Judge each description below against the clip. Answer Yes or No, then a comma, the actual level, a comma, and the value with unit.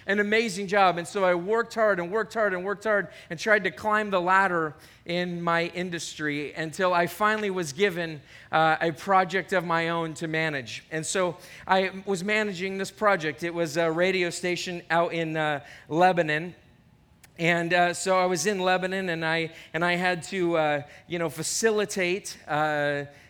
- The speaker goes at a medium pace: Yes, average, 180 wpm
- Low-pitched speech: No, medium, 175 Hz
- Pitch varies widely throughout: No, average, 3.0 semitones